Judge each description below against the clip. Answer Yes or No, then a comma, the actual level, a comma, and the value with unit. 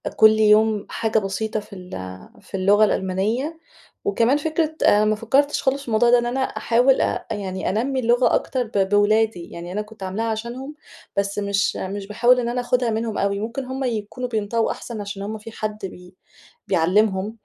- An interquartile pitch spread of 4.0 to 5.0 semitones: No, average, 3.2 semitones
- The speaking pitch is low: No, high, 220 Hz